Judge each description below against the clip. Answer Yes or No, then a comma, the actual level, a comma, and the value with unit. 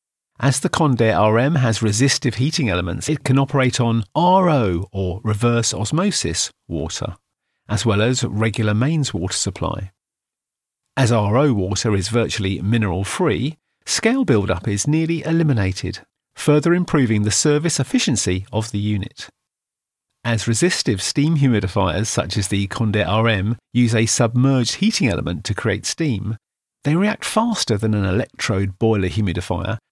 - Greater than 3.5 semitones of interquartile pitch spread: Yes, average, 5.1 semitones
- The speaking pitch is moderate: No, low, 115 Hz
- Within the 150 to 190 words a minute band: No, average, 140 wpm